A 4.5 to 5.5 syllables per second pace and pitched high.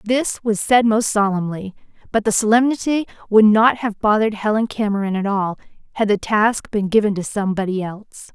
Yes: 5.4 syllables/s; high, 210 Hz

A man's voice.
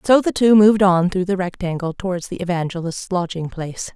No: female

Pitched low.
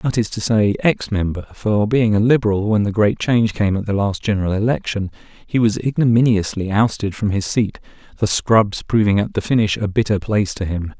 Yes: low, 105 Hz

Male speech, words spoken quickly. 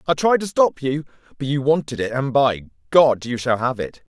Yes: male; fast, 230 wpm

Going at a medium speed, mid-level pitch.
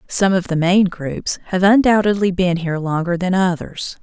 Yes: average, 180 wpm; medium, 180 Hz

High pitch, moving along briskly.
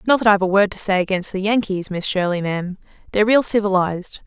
Yes: high, 195 Hz; fast, 225 wpm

